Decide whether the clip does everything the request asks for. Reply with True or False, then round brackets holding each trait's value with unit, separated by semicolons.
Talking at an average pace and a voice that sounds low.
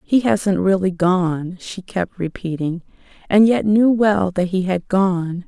False (165 wpm; 190 Hz)